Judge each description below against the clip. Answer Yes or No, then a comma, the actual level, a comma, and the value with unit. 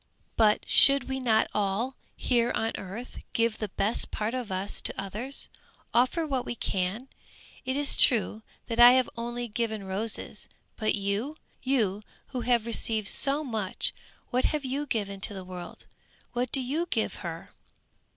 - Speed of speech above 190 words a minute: No, average, 160 wpm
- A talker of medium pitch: No, high, 230 Hz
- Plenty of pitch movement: No, average, 3.8 semitones